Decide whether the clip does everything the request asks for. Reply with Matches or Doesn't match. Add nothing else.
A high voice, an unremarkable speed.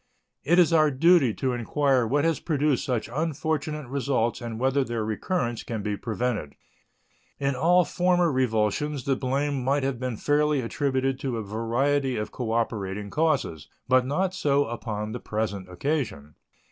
Doesn't match